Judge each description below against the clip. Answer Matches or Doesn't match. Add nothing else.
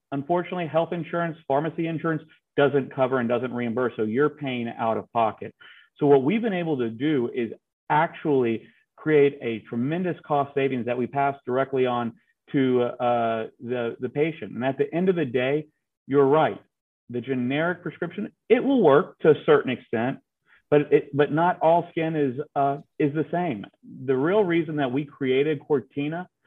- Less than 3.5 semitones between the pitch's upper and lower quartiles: Doesn't match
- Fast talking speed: Doesn't match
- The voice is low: Doesn't match